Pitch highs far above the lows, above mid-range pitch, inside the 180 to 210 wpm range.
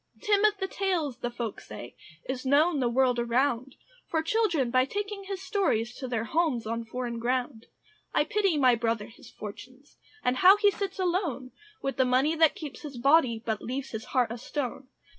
Yes: wide, 5.7 semitones; very high, 260 Hz; average, 190 wpm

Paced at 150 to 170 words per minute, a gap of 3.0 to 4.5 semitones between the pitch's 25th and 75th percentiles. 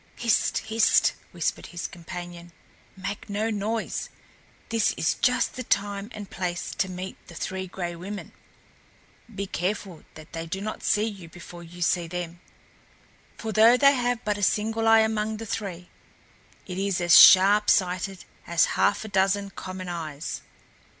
Yes: average, 155 wpm; average, 3.5 semitones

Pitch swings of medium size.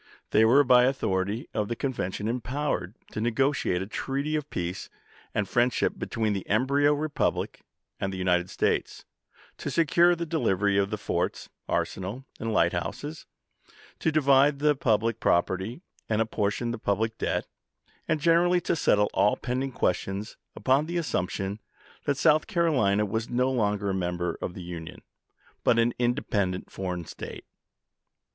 No: wide, 6.2 semitones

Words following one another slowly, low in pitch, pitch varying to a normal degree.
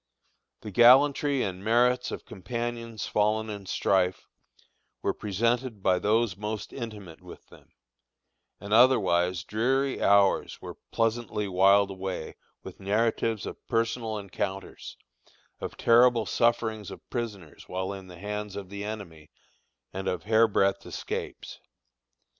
Yes: slow, 125 wpm; low, 105 Hz; average, 3.3 semitones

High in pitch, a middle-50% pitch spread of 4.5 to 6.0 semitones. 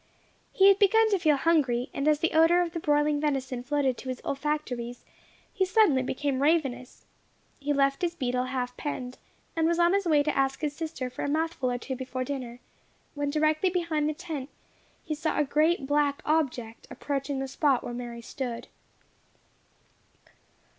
No: very high, 290 Hz; average, 3.7 semitones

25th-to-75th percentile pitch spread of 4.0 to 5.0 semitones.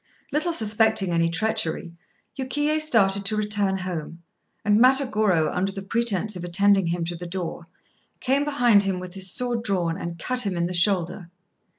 Yes: average, 4.5 semitones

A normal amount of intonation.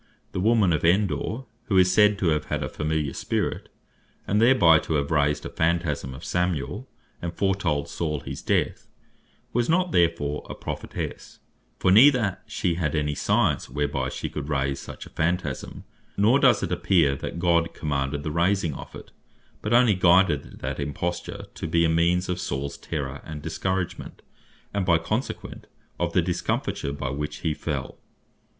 Yes: average, 4.4 semitones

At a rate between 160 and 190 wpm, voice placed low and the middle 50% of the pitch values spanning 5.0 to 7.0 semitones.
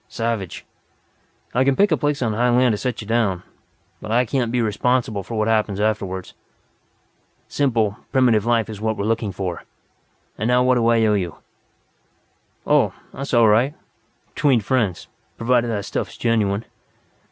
No: average, 165 wpm; low, 115 Hz; average, 2.9 semitones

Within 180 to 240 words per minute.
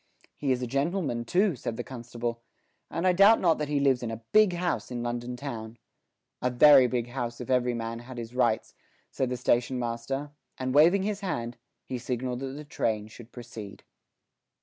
Yes: average, 195 wpm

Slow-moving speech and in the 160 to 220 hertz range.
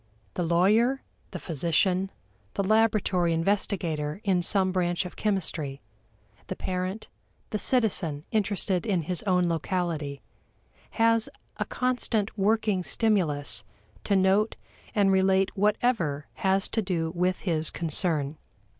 Yes: slow, 120 wpm; medium, 185 Hz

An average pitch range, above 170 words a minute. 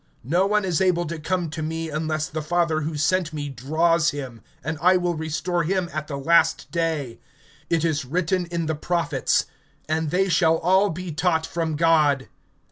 No: narrow, 2.2 semitones; average, 180 wpm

